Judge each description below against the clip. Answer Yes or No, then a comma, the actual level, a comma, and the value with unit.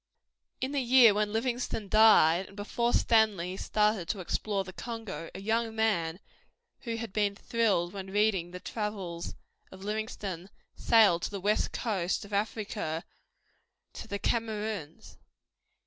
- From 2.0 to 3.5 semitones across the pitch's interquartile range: Yes, average, 2.9 semitones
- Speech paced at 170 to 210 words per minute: No, average, 140 wpm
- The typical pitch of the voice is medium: No, high, 210 Hz